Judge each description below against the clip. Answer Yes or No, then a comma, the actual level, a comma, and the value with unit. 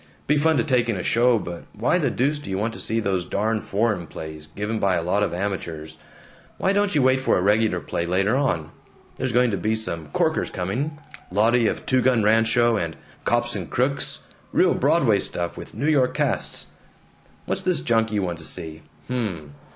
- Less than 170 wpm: No, fast, 205 wpm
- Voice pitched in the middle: No, low, 110 Hz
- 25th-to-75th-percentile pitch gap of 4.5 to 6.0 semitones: Yes, wide, 5.6 semitones